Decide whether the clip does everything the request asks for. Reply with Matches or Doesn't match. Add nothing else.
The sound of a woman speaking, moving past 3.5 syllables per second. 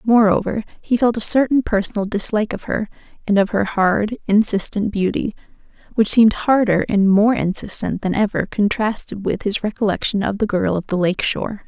Matches